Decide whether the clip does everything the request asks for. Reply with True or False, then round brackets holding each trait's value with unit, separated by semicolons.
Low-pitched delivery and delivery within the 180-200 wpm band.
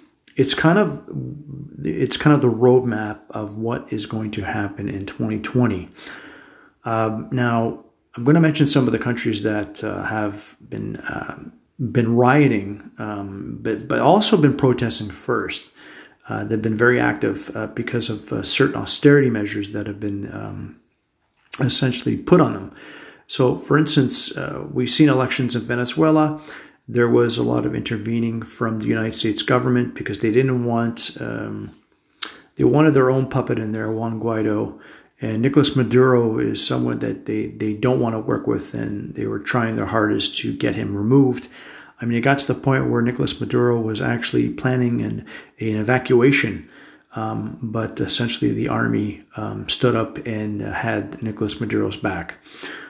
False (115 Hz; 165 wpm)